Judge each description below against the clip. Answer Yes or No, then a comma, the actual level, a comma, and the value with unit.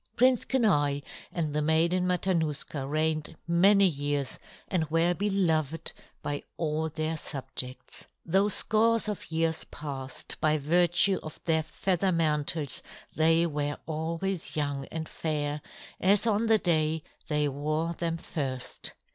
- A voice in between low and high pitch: Yes, medium, 160 Hz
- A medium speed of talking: No, slow, 130 wpm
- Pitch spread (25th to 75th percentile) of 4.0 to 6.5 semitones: No, average, 3.1 semitones